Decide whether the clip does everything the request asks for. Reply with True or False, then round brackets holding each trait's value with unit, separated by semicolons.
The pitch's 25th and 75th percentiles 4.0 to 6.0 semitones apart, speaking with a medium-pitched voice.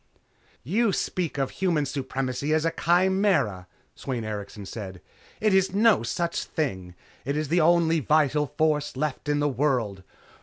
True (5.1 semitones; 150 Hz)